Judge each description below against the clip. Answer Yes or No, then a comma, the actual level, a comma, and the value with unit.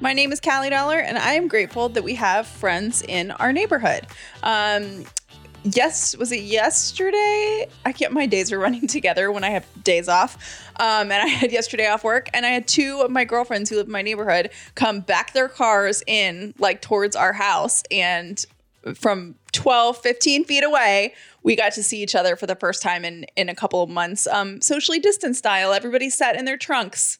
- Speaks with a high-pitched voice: Yes, high, 220 Hz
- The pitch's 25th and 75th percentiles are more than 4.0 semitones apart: Yes, average, 5.0 semitones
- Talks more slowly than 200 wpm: No, fast, 205 wpm